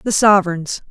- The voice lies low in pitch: No, high, 190 Hz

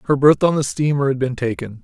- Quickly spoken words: Yes, fast, 260 wpm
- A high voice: No, low, 135 Hz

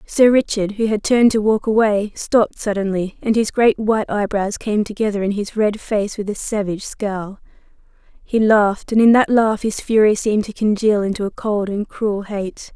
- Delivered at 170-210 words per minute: Yes, average, 200 wpm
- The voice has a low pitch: No, high, 210 Hz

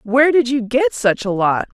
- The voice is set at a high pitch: Yes, high, 245 Hz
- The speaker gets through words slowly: No, fast, 235 wpm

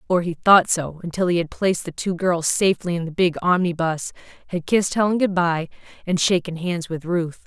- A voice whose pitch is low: No, medium, 175 Hz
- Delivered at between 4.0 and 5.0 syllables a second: No, 5.4 syllables/s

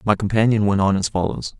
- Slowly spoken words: No, fast, 225 wpm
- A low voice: Yes, low, 100 Hz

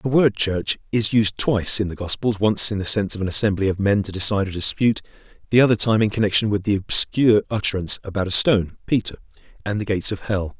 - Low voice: Yes, low, 100 Hz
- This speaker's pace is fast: Yes, fast, 215 wpm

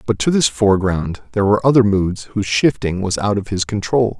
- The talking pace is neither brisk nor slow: No, fast, 215 wpm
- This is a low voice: Yes, low, 105 Hz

